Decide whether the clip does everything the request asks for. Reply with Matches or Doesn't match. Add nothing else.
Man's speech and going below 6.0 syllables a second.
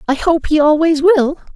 Doesn't match